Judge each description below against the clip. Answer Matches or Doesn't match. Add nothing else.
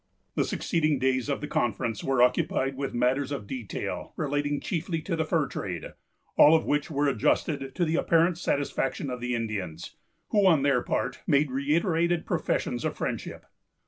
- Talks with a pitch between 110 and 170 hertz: Matches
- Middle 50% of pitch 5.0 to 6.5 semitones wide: Doesn't match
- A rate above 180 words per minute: Doesn't match